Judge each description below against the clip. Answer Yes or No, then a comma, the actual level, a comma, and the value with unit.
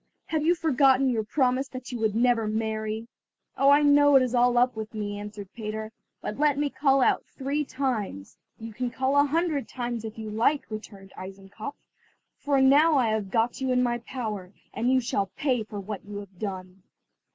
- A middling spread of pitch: Yes, average, 4.1 semitones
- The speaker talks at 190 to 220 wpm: Yes, average, 195 wpm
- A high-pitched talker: Yes, high, 240 Hz